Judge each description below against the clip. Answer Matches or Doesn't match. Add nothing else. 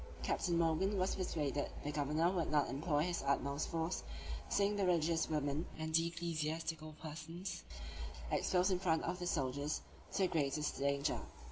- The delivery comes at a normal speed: Matches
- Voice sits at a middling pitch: Matches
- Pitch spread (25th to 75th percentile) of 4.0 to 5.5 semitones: Doesn't match